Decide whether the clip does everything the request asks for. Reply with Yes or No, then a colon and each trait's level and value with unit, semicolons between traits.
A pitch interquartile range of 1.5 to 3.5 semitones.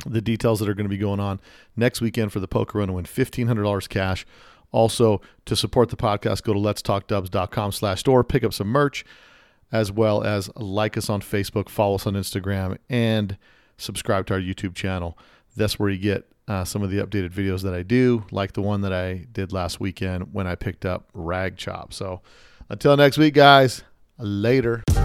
Yes: average, 2.8 semitones